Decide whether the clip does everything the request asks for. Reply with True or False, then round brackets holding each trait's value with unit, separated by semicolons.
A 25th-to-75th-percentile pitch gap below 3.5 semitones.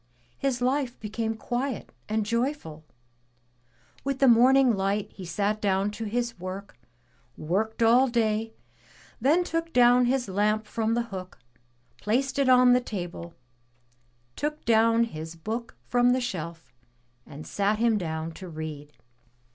False (4.3 semitones)